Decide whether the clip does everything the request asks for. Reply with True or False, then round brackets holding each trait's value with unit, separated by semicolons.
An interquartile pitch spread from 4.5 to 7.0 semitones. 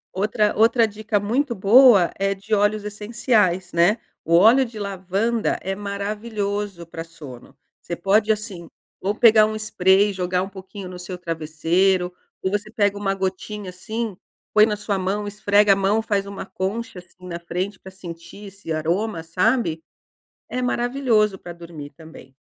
False (2.9 semitones)